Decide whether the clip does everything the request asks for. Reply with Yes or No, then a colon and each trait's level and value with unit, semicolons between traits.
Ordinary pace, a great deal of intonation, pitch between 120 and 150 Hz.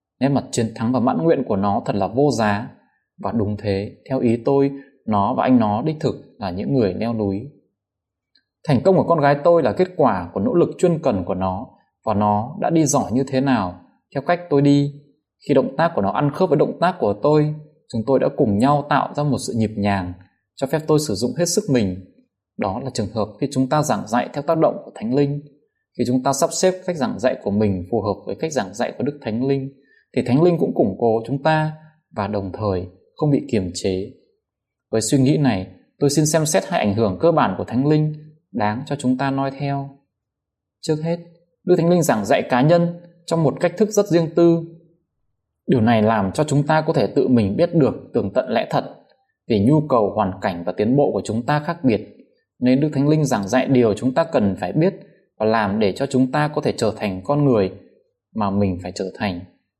Yes: average, 235 wpm; wide, 6.6 semitones; low, 135 Hz